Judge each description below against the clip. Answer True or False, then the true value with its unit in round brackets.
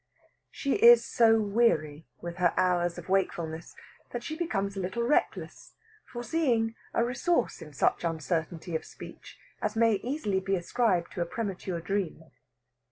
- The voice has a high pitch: True (195 Hz)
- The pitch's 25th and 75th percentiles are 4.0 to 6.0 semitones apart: True (5.4 semitones)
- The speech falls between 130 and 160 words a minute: True (150 wpm)